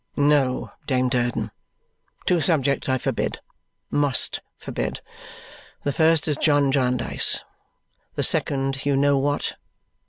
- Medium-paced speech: No, slow, 115 wpm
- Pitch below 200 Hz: Yes, medium, 140 Hz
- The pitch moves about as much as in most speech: No, narrow, 1.8 semitones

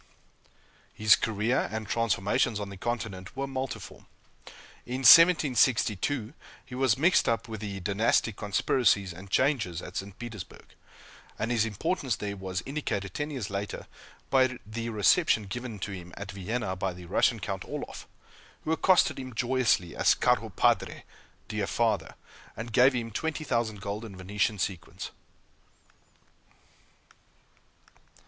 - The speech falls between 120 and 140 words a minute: Yes, slow, 135 wpm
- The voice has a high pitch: No, low, 110 Hz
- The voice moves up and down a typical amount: Yes, average, 4.4 semitones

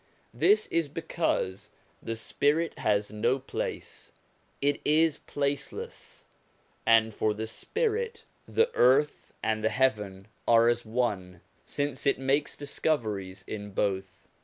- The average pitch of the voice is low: Yes, low, 120 Hz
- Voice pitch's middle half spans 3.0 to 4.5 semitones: No, wide, 5.5 semitones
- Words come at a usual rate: No, slow, 120 wpm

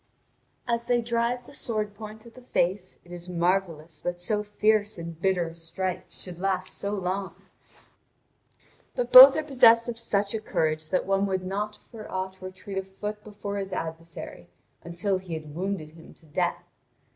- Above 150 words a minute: Yes, average, 170 wpm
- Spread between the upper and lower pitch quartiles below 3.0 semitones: No, average, 3.5 semitones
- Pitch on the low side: No, high, 195 Hz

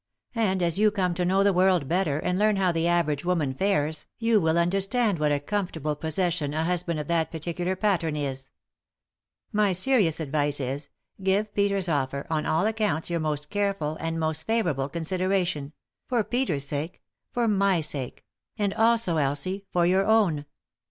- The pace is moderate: Yes, average, 175 wpm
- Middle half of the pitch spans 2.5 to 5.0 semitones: Yes, average, 4.4 semitones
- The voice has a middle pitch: Yes, medium, 175 Hz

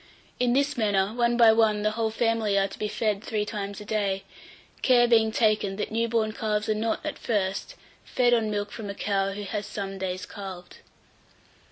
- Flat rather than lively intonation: Yes, narrow, 2.3 semitones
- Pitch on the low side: No, high, 215 Hz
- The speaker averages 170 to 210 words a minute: Yes, average, 200 wpm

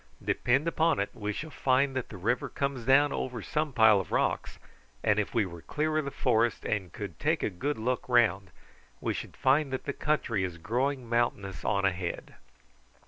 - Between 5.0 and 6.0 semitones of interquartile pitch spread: Yes, wide, 5.5 semitones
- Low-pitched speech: Yes, low, 120 Hz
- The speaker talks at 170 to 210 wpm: Yes, average, 195 wpm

